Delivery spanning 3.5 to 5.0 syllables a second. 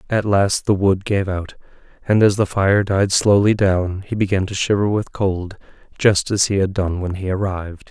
Yes: 4.7 syllables/s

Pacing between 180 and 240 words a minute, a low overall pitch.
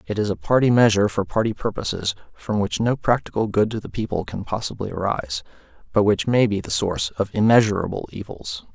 Yes: average, 190 wpm; low, 100 Hz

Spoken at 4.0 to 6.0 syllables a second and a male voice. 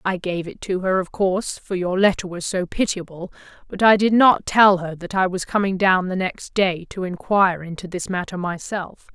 No: 5.0 syllables/s; female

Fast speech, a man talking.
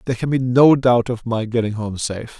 Yes: fast, 250 wpm; male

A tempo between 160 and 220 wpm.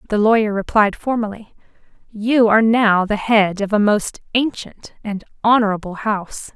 No: average, 145 wpm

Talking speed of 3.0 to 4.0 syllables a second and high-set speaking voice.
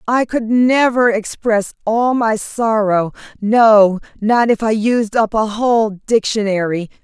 Yes: 3.7 syllables/s; high, 220 Hz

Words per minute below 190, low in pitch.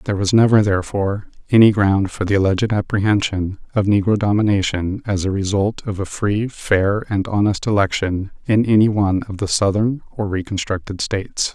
Yes: average, 165 wpm; low, 100 Hz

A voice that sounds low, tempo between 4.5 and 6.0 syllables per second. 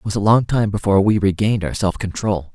No: low, 100 Hz; 6.4 syllables/s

